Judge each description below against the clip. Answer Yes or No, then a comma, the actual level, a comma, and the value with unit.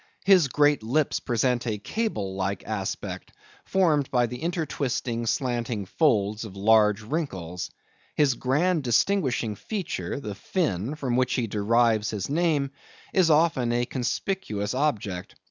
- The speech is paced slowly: Yes, slow, 130 wpm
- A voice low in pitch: Yes, low, 125 Hz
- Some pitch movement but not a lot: No, wide, 6.0 semitones